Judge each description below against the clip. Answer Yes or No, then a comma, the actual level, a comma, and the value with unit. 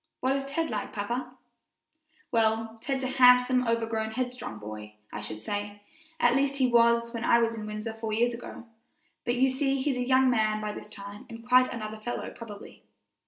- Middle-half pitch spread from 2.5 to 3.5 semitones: Yes, average, 2.8 semitones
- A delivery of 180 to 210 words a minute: Yes, average, 190 wpm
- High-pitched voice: Yes, high, 235 Hz